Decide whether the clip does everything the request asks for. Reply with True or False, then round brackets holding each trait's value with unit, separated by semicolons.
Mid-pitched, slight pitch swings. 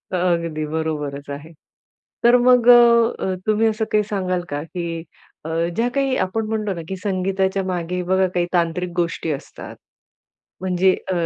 False (180 Hz; 3.5 semitones)